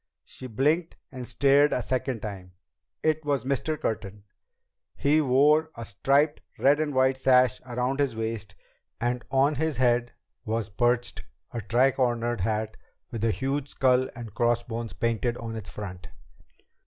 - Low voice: Yes, low, 125 Hz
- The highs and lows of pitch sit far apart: No, average, 3.3 semitones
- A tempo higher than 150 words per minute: No, average, 145 wpm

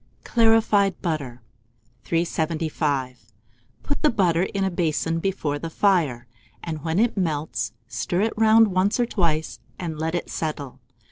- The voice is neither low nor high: Yes, medium, 165 Hz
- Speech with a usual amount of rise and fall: Yes, average, 4.4 semitones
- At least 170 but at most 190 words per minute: No, average, 140 wpm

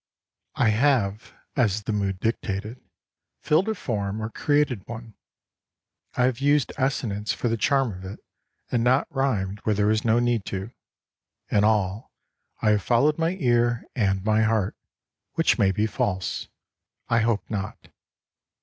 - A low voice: Yes, low, 110 Hz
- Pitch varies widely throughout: No, average, 3.4 semitones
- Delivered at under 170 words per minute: Yes, average, 150 wpm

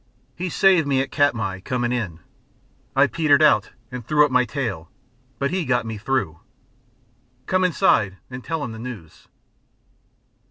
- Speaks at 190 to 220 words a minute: No, average, 155 wpm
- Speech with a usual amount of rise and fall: Yes, average, 4.9 semitones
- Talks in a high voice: No, low, 125 Hz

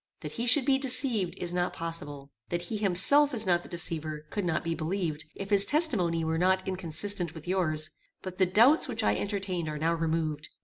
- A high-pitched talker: No, medium, 175 Hz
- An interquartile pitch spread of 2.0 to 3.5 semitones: No, average, 3.9 semitones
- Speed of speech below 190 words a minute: No, fast, 205 wpm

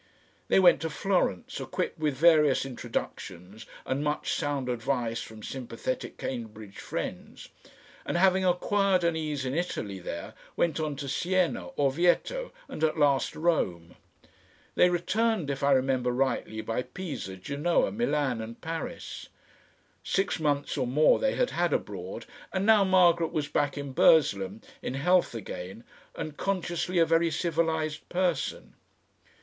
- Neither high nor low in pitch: Yes, medium, 150 Hz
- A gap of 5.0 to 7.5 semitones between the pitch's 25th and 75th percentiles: Yes, wide, 5.4 semitones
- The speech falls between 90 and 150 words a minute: Yes, average, 140 wpm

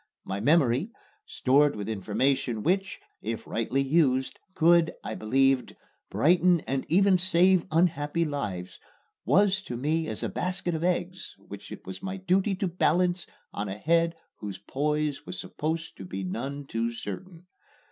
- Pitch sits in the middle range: Yes, medium, 150 Hz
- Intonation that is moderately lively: No, wide, 6.1 semitones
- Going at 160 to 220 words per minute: No, average, 150 wpm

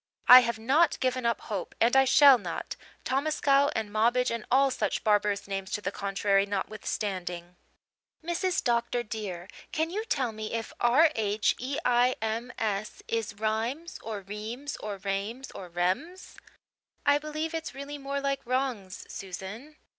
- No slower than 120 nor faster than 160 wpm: Yes, average, 155 wpm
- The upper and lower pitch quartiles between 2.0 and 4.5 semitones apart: No, average, 5.0 semitones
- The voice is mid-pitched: No, high, 230 Hz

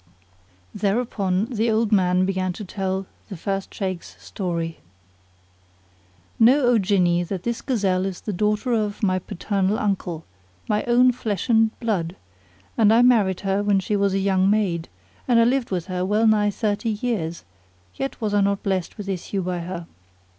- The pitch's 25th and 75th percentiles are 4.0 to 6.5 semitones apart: No, average, 2.8 semitones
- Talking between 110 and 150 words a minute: No, average, 170 wpm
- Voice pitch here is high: Yes, high, 200 Hz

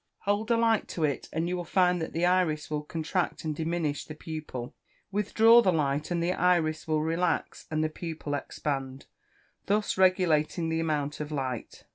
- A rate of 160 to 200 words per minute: Yes, average, 180 wpm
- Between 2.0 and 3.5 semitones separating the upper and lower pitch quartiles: Yes, average, 3.1 semitones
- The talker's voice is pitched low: No, medium, 160 Hz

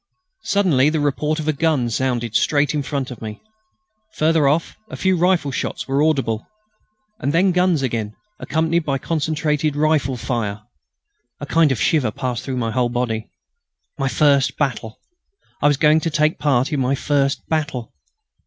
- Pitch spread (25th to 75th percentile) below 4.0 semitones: Yes, average, 3.6 semitones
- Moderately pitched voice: Yes, medium, 145 Hz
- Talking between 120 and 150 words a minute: No, average, 165 wpm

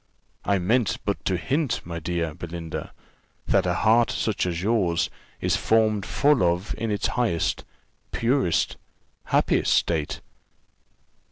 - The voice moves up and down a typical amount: Yes, average, 4.9 semitones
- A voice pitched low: Yes, very low, 95 Hz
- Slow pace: Yes, slow, 125 wpm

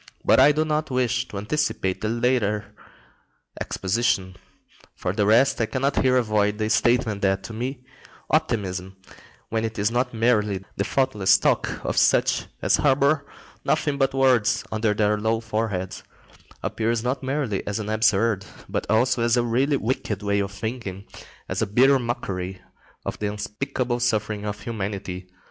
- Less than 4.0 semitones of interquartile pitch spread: Yes, average, 3.6 semitones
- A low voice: Yes, low, 110 Hz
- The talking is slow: No, average, 160 wpm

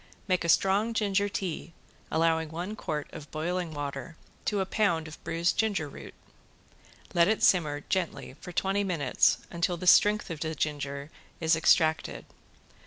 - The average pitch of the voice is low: No, medium, 170 Hz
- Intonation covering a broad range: No, average, 3.4 semitones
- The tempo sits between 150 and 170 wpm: Yes, average, 155 wpm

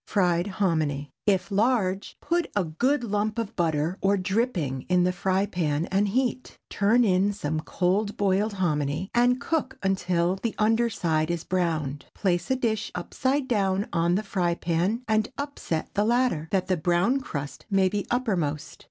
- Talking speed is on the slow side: No, average, 165 wpm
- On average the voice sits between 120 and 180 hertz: No, high, 190 Hz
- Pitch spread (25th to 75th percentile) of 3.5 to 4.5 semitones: Yes, average, 4.2 semitones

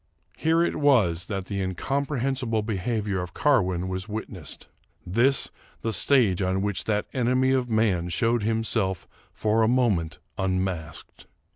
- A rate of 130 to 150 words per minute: Yes, average, 140 wpm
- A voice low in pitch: Yes, low, 110 Hz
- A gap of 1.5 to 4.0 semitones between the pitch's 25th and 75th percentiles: No, average, 4.9 semitones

